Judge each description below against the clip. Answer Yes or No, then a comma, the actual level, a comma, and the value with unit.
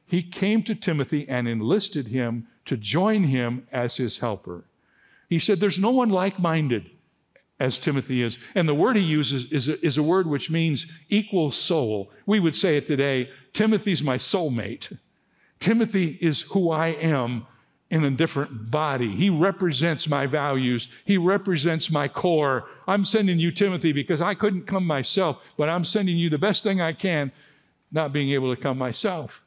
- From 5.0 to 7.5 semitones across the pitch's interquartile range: Yes, wide, 5.5 semitones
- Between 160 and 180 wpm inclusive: Yes, average, 175 wpm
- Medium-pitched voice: Yes, medium, 160 Hz